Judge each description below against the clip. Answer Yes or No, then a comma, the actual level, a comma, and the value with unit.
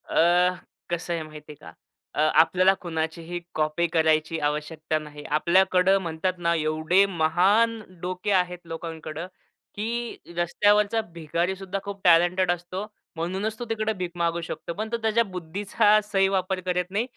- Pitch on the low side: No, medium, 180 Hz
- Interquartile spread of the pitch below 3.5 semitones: Yes, average, 3.1 semitones